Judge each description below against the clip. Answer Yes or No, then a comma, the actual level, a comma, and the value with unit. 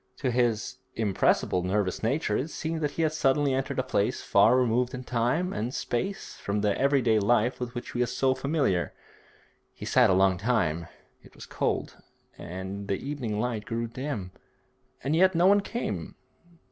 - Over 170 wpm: Yes, average, 180 wpm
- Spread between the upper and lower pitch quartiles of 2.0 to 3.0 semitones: No, average, 5.0 semitones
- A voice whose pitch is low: Yes, low, 120 Hz